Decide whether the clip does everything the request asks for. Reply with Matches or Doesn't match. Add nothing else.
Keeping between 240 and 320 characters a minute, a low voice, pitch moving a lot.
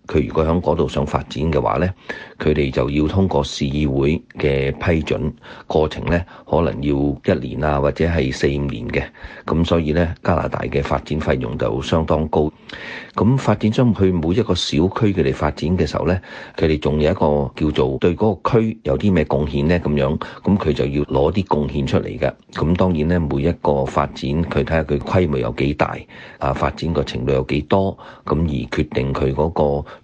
Doesn't match